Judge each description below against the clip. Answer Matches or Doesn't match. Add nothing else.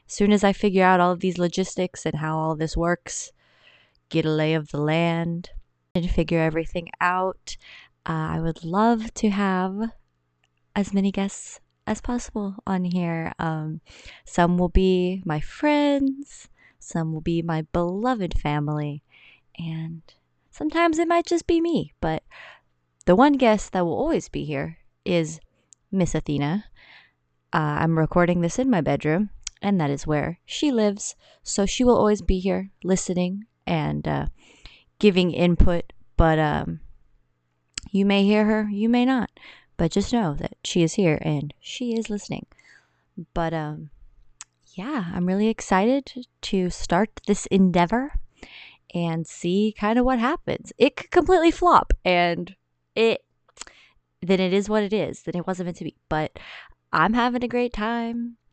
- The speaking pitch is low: Doesn't match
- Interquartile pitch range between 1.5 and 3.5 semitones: Doesn't match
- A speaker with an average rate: Matches